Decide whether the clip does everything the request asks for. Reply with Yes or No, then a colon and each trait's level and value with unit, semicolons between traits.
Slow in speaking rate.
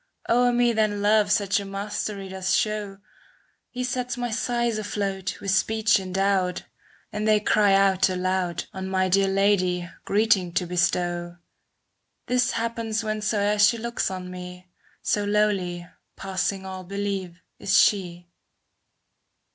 Yes: slow, 130 wpm